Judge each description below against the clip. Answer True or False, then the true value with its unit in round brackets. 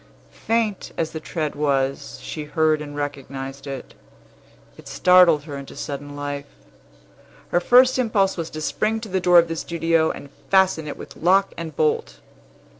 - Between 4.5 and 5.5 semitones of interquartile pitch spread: False (4.0 semitones)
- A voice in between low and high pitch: True (160 Hz)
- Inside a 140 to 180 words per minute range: True (165 wpm)